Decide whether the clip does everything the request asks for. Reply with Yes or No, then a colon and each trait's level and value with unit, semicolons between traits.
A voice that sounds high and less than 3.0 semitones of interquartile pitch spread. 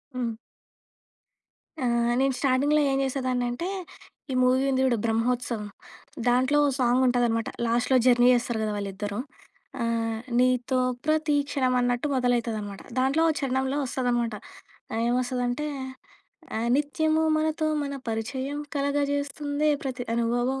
Yes: very high, 250 Hz; narrow, 2.6 semitones